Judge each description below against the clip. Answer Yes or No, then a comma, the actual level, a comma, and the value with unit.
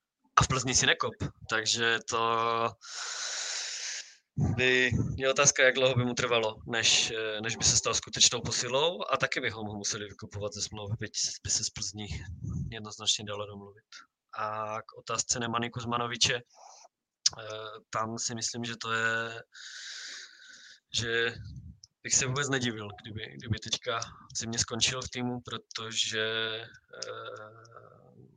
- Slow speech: No, average, 125 wpm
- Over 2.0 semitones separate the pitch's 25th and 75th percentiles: Yes, average, 2.9 semitones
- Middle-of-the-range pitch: No, low, 115 Hz